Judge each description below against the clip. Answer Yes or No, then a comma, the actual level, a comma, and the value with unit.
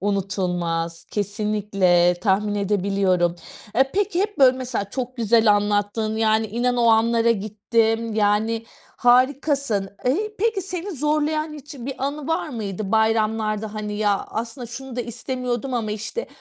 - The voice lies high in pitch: Yes, high, 225 Hz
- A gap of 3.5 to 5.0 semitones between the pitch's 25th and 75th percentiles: Yes, average, 4.0 semitones